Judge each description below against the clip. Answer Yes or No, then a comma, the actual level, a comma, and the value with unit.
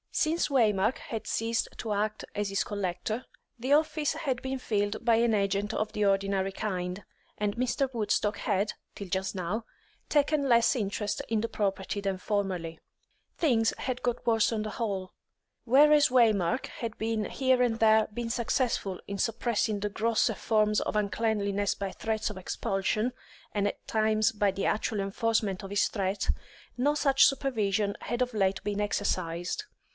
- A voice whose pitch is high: Yes, high, 215 Hz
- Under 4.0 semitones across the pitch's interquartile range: Yes, average, 2.9 semitones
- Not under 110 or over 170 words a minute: Yes, average, 160 wpm